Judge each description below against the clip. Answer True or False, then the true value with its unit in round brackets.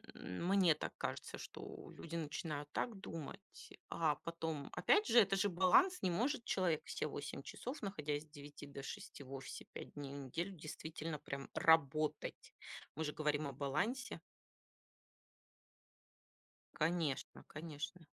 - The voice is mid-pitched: True (160 Hz)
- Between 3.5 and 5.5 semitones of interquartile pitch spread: True (4.2 semitones)